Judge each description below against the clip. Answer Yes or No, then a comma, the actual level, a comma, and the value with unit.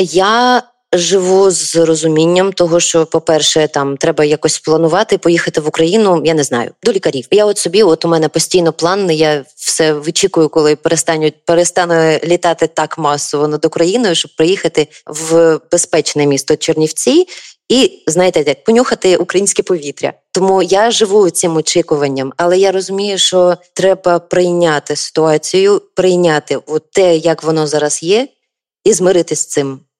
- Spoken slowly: No, average, 145 wpm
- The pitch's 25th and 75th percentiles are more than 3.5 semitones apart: No, average, 3.0 semitones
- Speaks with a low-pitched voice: No, medium, 165 Hz